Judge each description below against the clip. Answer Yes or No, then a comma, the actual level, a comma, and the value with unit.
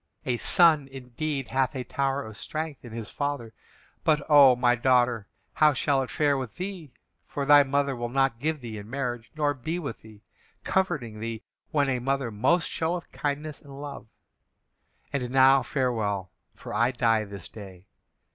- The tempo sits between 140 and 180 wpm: Yes, average, 170 wpm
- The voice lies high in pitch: No, low, 135 Hz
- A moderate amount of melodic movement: Yes, average, 3.6 semitones